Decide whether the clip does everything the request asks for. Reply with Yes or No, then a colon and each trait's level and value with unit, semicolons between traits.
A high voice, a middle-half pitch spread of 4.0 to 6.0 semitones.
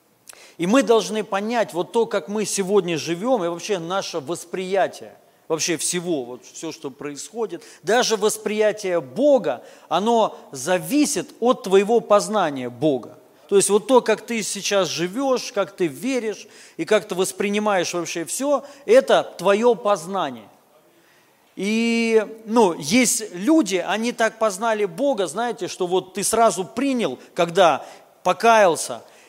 Yes: high, 205 Hz; average, 4.3 semitones